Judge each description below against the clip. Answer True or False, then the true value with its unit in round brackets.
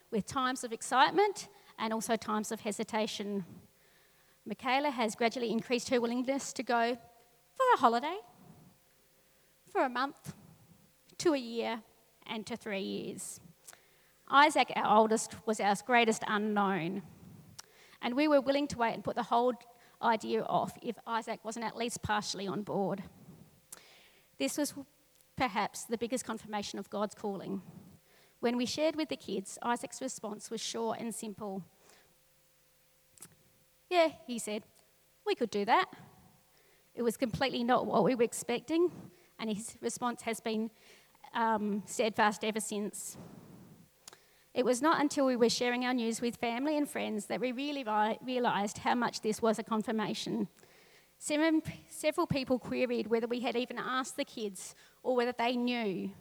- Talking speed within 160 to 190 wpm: False (150 wpm)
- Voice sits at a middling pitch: False (230 Hz)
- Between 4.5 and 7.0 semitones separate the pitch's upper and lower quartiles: False (3.0 semitones)